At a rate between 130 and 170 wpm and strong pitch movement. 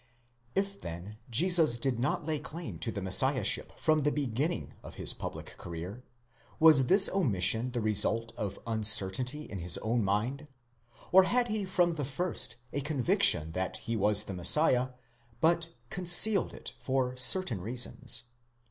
Yes: average, 150 wpm; wide, 7.0 semitones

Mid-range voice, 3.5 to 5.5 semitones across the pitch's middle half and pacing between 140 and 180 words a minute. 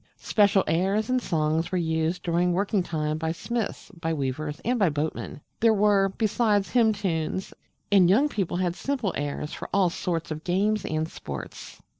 Yes: medium, 180 Hz; average, 4.3 semitones; average, 170 wpm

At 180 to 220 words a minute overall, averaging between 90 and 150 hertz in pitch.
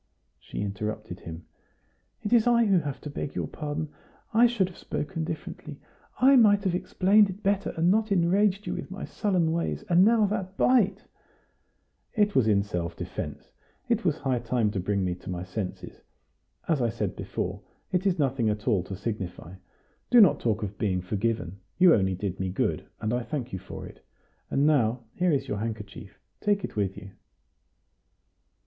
Yes: average, 185 wpm; medium, 140 Hz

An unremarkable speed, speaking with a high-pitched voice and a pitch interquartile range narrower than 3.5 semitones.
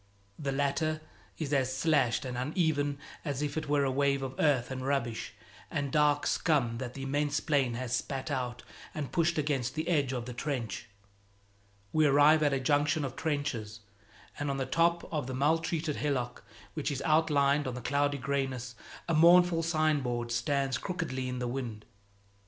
No: average, 175 wpm; medium, 140 Hz; average, 2.9 semitones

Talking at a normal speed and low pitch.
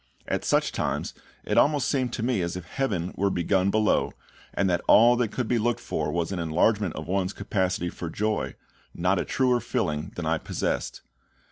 Yes: average, 195 wpm; very low, 95 Hz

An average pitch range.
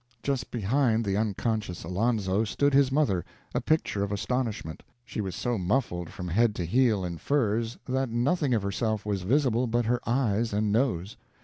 Yes: average, 4.2 semitones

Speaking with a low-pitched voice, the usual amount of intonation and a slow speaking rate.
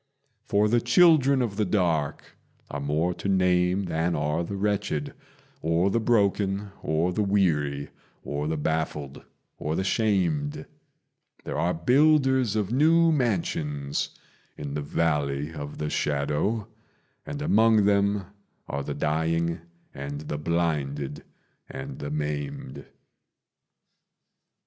No: very low, 85 Hz; wide, 5.8 semitones; slow, 120 wpm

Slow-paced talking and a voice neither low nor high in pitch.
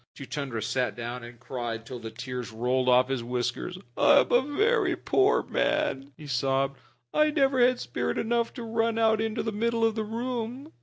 No: average, 190 wpm; medium, 150 Hz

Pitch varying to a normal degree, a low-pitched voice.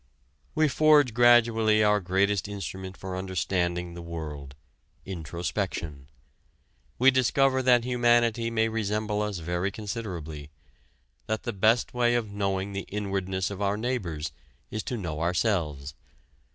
Yes: average, 4.7 semitones; low, 100 Hz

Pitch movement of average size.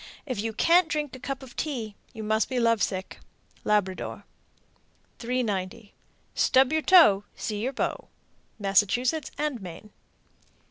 Yes: average, 4.6 semitones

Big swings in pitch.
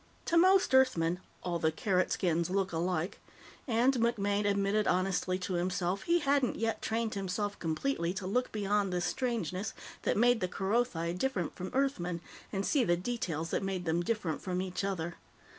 No: average, 4.4 semitones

